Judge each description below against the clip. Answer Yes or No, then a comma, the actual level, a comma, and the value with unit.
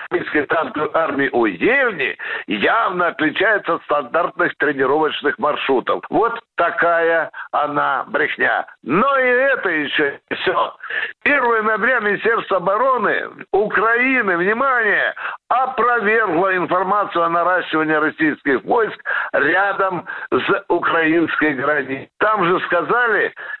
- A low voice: No, high, 200 Hz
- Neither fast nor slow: No, slow, 100 wpm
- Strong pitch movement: Yes, wide, 6.8 semitones